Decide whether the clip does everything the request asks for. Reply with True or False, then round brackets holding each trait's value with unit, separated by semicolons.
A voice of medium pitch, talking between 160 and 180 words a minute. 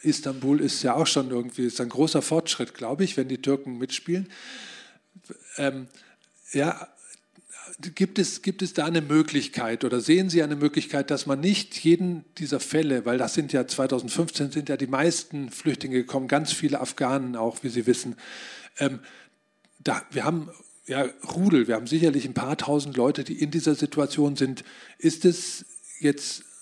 True (145 Hz; 170 wpm)